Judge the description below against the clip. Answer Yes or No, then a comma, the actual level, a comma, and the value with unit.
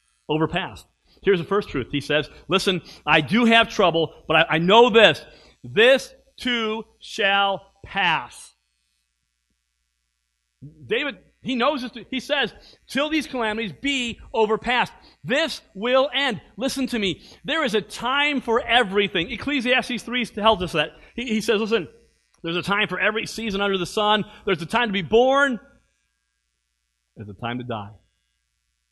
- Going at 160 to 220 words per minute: No, average, 150 wpm